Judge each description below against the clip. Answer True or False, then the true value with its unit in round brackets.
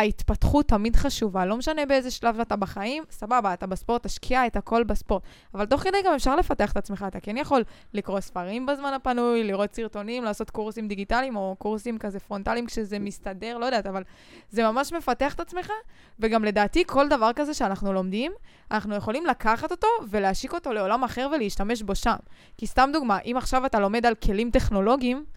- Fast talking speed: True (185 wpm)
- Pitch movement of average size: True (4.3 semitones)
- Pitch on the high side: True (230 Hz)